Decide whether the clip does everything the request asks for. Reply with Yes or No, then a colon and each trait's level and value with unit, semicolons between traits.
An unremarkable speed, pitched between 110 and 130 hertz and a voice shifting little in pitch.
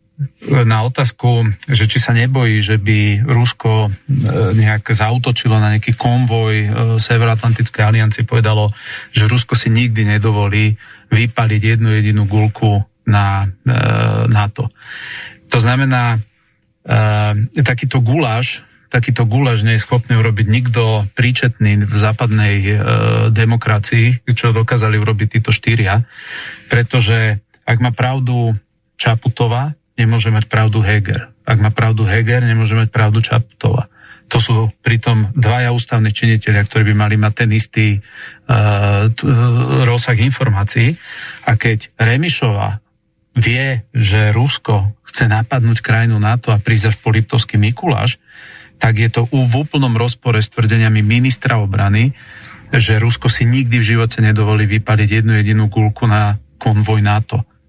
Yes: average, 130 wpm; low, 115 Hz; narrow, 2.2 semitones